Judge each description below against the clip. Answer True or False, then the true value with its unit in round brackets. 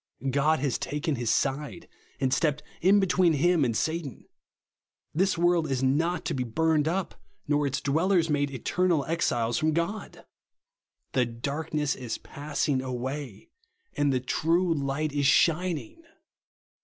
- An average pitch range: True (3.6 semitones)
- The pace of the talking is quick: False (145 wpm)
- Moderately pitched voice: True (150 Hz)